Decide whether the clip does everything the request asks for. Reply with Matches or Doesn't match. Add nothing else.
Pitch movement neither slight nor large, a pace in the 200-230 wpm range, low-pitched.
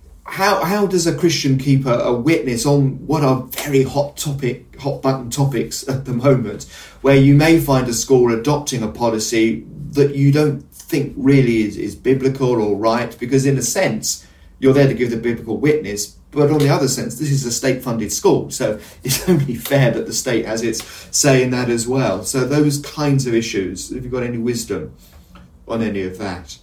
Matches